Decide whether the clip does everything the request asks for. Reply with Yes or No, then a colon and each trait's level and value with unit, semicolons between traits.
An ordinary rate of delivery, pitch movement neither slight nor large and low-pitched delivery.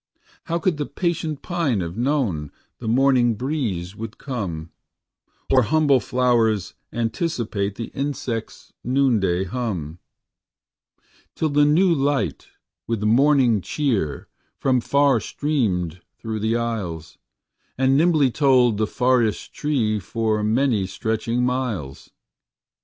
No: slow, 115 wpm; average, 4.7 semitones; low, 120 Hz